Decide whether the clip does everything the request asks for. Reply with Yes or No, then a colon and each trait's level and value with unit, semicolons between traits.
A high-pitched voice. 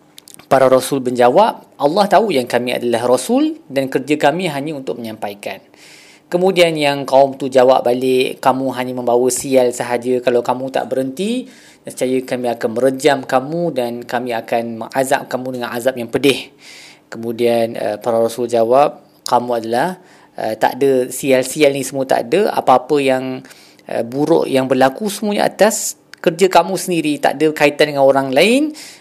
No: low, 130 Hz